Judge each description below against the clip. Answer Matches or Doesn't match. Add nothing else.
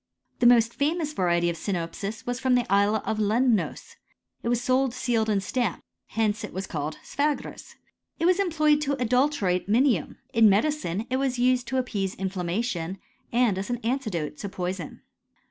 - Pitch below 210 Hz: Doesn't match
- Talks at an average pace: Matches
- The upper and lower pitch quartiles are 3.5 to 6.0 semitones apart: Matches